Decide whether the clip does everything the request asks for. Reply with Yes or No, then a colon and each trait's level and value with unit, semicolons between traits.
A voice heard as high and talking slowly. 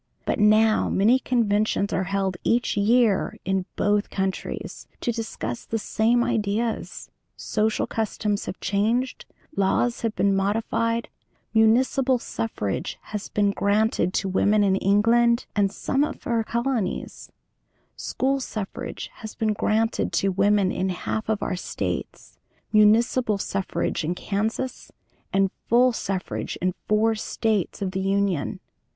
Yes: high, 215 Hz; slow, 130 wpm